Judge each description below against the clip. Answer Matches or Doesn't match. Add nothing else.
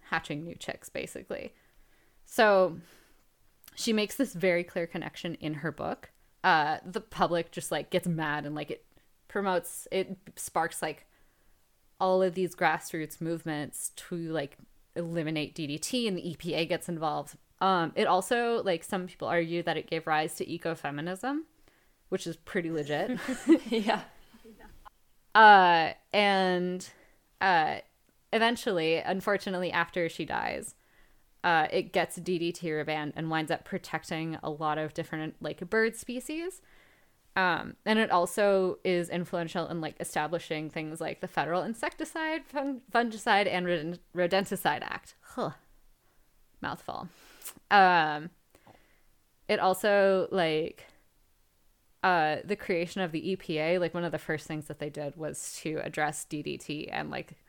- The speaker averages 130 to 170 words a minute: Matches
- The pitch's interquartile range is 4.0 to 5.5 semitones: Doesn't match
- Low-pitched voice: Doesn't match